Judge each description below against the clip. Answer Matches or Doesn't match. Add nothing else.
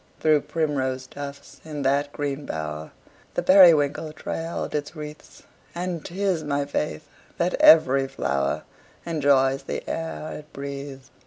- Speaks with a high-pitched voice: Doesn't match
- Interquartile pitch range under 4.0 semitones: Matches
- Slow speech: Matches